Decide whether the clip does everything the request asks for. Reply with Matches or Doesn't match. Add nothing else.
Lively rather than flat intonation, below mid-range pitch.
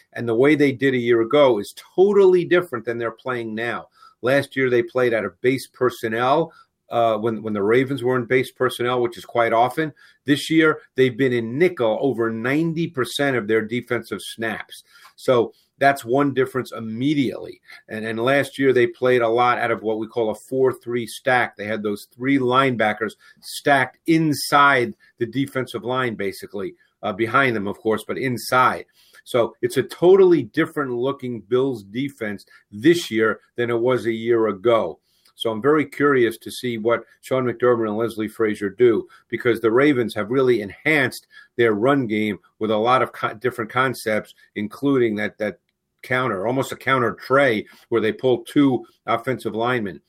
Doesn't match